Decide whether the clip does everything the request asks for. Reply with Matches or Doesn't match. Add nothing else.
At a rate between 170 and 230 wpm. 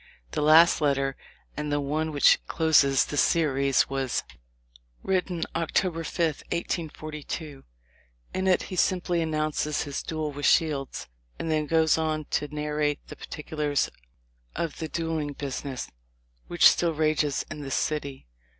Doesn't match